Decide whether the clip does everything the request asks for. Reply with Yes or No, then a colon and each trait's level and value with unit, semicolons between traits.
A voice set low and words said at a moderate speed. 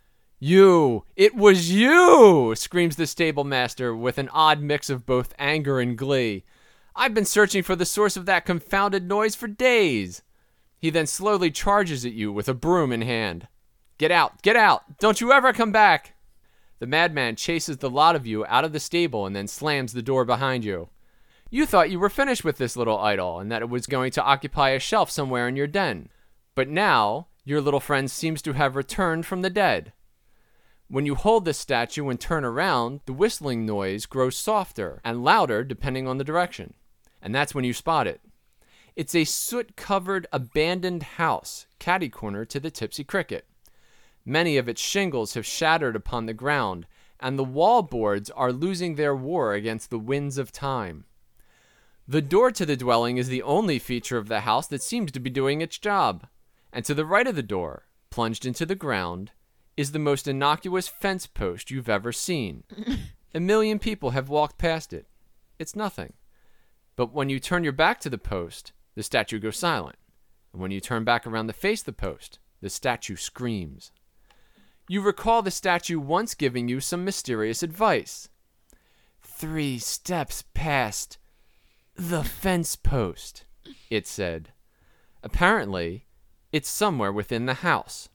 No: medium, 145 Hz; average, 175 wpm